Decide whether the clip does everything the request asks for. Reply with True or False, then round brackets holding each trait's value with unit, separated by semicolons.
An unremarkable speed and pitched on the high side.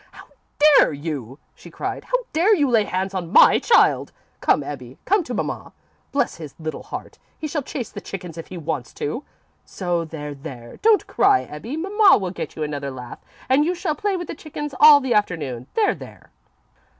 True (195 wpm; 200 Hz)